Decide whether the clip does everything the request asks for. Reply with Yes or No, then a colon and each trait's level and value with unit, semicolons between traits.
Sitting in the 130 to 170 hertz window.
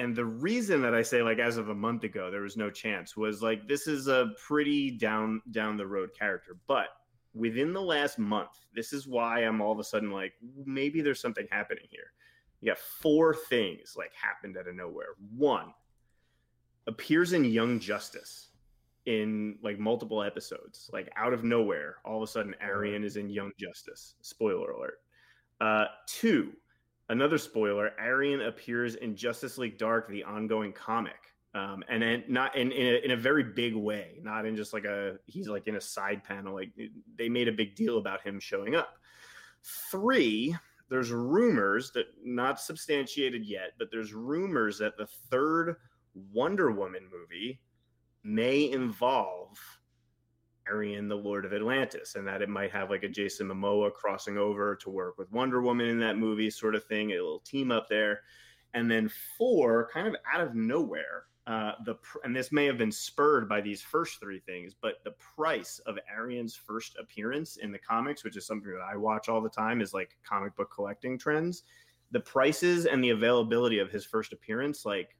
No: low, 115 Hz